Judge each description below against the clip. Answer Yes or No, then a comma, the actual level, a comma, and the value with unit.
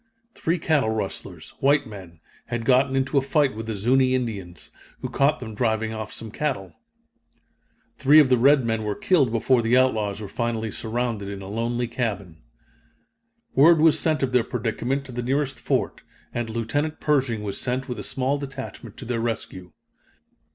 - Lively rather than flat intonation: No, average, 3.6 semitones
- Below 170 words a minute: No, average, 175 wpm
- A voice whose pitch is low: Yes, low, 120 Hz